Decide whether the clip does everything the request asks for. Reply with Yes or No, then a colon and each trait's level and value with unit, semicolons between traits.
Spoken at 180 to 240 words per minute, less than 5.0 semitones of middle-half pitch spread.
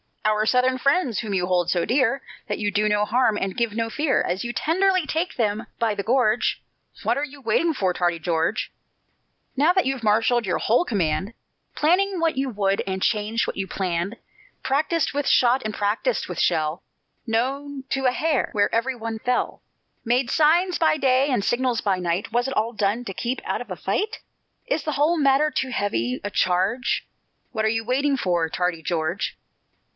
No: average, 190 wpm; average, 5.3 semitones